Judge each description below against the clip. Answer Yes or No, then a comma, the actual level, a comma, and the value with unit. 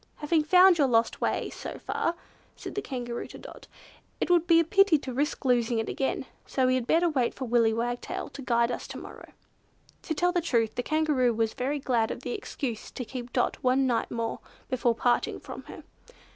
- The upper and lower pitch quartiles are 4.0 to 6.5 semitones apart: Yes, average, 4.5 semitones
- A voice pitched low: No, very high, 255 Hz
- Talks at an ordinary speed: No, fast, 210 wpm